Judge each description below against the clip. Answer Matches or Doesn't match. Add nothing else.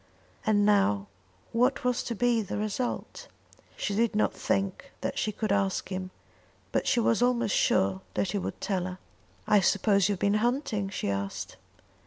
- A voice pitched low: Doesn't match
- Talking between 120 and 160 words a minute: Doesn't match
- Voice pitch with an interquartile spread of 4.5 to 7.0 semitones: Doesn't match